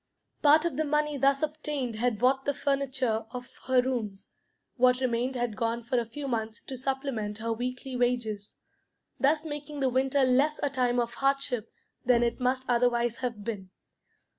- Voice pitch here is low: No, very high, 255 Hz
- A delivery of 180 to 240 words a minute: No, average, 170 wpm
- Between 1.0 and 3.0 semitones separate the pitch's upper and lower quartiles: Yes, narrow, 2.6 semitones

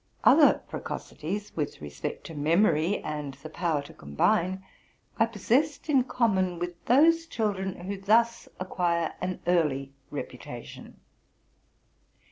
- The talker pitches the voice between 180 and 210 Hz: Yes, medium, 185 Hz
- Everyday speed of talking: No, slow, 115 wpm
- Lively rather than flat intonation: Yes, wide, 5.7 semitones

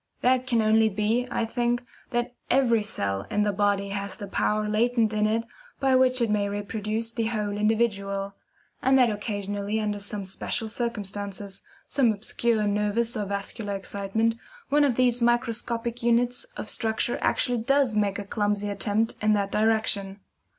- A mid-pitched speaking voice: No, high, 215 Hz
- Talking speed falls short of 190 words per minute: Yes, average, 160 wpm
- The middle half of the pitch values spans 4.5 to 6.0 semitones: No, narrow, 2.6 semitones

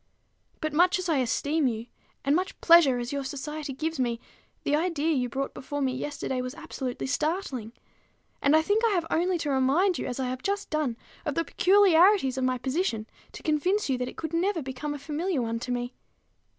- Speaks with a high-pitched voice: Yes, very high, 290 Hz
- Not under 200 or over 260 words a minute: Yes, fast, 205 wpm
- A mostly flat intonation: No, average, 4.6 semitones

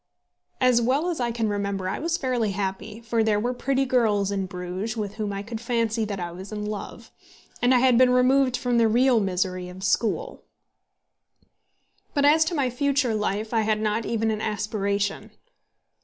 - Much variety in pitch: No, average, 3.7 semitones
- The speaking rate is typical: Yes, average, 185 wpm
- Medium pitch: No, high, 220 Hz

